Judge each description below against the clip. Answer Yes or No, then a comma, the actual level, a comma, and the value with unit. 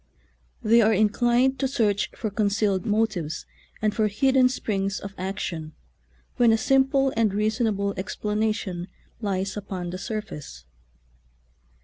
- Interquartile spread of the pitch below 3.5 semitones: Yes, average, 2.9 semitones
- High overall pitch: Yes, high, 210 Hz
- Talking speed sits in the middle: No, slow, 130 wpm